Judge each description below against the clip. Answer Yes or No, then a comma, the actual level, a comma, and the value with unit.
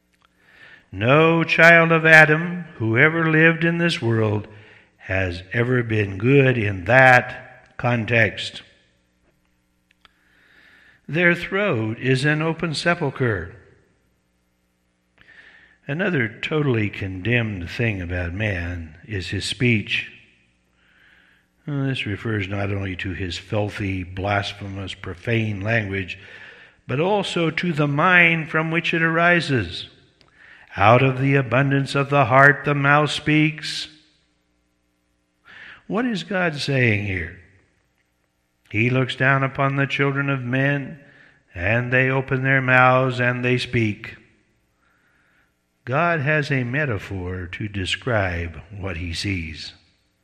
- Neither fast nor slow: No, slow, 110 wpm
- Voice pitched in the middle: No, low, 115 Hz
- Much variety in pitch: Yes, wide, 6.9 semitones